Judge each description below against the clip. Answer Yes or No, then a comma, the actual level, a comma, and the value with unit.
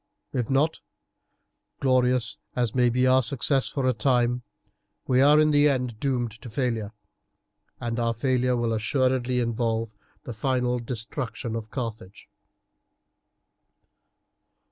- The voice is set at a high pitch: No, low, 125 Hz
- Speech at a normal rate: No, slow, 120 wpm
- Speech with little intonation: Yes, narrow, 2.1 semitones